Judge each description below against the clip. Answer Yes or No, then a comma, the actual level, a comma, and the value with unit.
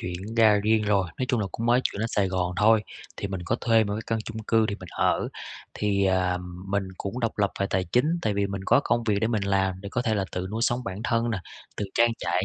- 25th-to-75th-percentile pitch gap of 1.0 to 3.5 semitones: Yes, average, 3.0 semitones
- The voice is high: No, low, 105 Hz